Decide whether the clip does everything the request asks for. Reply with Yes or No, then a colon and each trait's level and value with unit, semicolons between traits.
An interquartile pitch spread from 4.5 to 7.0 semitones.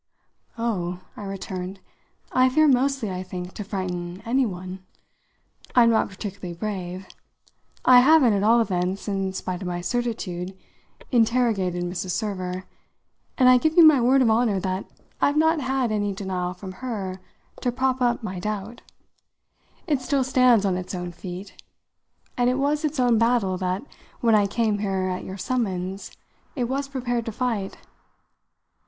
Yes: average, 5.0 semitones